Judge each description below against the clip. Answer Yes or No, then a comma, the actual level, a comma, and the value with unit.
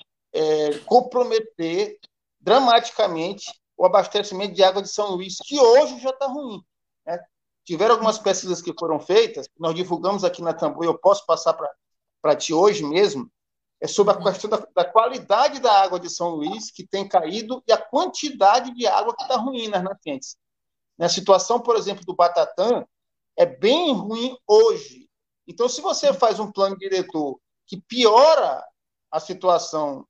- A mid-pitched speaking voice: No, high, 200 Hz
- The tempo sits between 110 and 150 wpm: No, average, 160 wpm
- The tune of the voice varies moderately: No, wide, 5.9 semitones